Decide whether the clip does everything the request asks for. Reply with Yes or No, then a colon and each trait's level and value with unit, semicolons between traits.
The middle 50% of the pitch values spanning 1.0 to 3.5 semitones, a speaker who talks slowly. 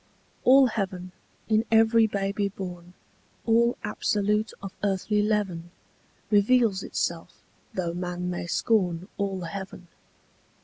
Yes: average, 3.2 semitones; slow, 105 wpm